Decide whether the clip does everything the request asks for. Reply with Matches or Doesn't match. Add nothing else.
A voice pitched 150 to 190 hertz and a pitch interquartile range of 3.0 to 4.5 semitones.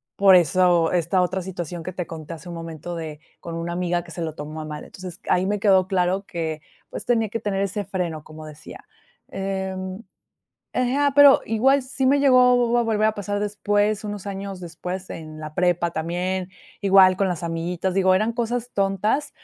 Matches